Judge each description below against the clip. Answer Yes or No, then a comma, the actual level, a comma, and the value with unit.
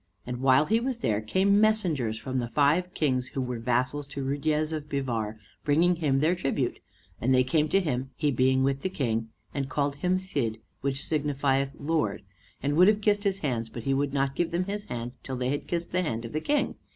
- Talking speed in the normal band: No, fast, 220 wpm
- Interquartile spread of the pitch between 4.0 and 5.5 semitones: Yes, average, 4.7 semitones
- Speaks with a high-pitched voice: No, medium, 140 Hz